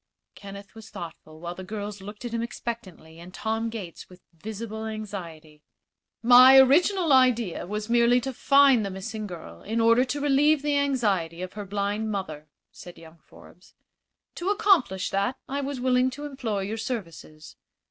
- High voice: Yes, high, 220 Hz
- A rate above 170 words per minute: No, average, 165 wpm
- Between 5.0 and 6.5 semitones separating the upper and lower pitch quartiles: Yes, average, 5.3 semitones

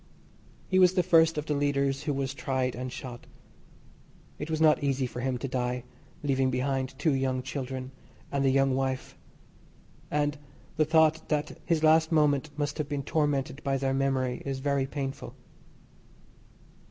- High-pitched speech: No, medium, 140 Hz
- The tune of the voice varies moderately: No, narrow, 2.2 semitones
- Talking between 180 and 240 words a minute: No, average, 165 wpm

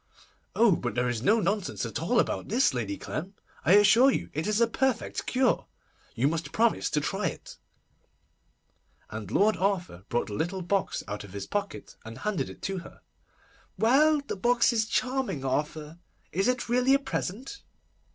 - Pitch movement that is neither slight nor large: No, wide, 8.1 semitones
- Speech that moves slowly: No, average, 175 wpm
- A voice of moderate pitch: No, high, 200 Hz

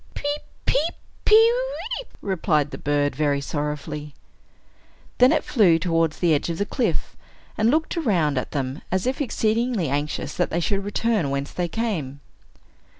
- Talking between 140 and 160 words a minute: Yes, average, 155 wpm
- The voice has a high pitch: No, medium, 175 Hz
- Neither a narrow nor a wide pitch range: No, wide, 8.0 semitones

